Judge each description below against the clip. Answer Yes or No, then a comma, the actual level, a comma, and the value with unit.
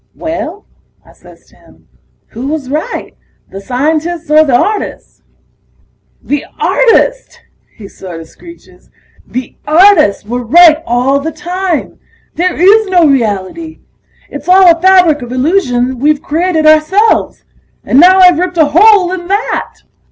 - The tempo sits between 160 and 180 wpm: No, slow, 135 wpm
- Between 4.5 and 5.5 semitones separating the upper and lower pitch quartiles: Yes, average, 5.2 semitones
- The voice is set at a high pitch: Yes, very high, 320 Hz